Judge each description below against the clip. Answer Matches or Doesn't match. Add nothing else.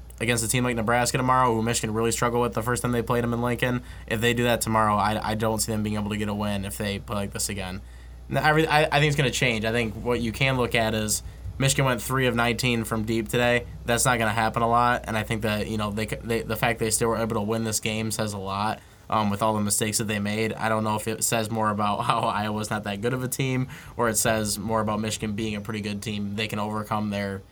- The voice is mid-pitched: Doesn't match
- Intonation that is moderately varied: Doesn't match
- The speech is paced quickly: Matches